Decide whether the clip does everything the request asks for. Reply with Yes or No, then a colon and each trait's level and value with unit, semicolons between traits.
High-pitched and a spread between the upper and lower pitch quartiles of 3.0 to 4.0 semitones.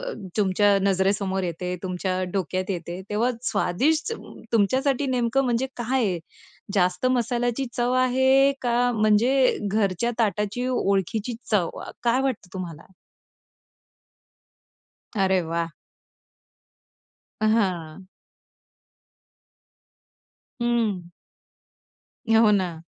No: high, 210 Hz; average, 4.7 semitones